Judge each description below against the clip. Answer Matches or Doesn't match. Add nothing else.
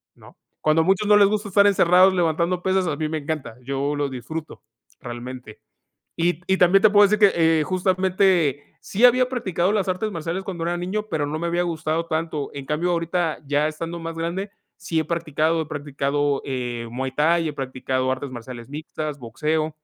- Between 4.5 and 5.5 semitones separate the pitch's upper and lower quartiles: Doesn't match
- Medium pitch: Matches